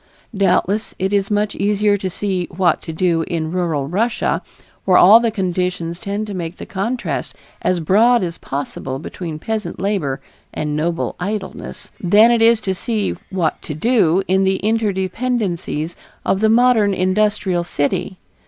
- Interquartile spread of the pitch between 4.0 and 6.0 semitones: No, average, 3.5 semitones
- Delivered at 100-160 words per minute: Yes, average, 155 wpm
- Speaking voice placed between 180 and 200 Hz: Yes, high, 190 Hz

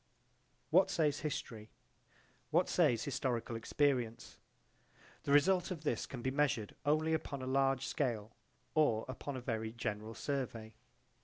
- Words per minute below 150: Yes, slow, 135 wpm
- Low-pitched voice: Yes, low, 130 Hz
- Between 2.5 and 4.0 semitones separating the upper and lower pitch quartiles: No, average, 4.4 semitones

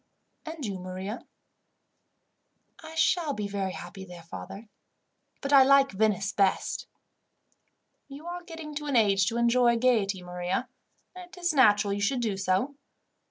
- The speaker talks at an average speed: Yes, average, 150 wpm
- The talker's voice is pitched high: Yes, high, 230 Hz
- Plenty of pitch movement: Yes, wide, 6.4 semitones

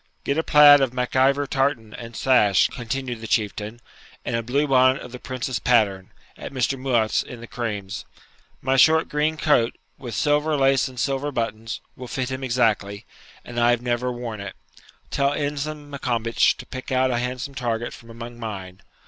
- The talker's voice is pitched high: No, low, 125 Hz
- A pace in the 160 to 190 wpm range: Yes, average, 180 wpm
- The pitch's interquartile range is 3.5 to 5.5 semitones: No, average, 2.9 semitones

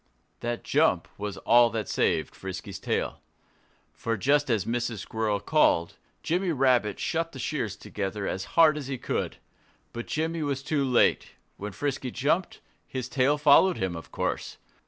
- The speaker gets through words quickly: No, average, 155 wpm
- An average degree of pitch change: No, wide, 5.9 semitones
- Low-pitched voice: Yes, low, 125 Hz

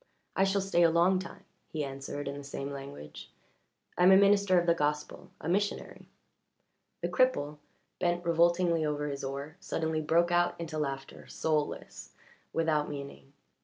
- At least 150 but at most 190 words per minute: Yes, average, 160 wpm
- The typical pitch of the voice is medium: Yes, medium, 160 Hz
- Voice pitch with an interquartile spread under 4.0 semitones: Yes, average, 3.3 semitones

